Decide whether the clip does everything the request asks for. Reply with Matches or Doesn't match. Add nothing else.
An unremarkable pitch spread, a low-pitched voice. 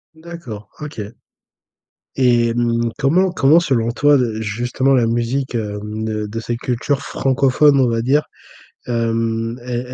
Matches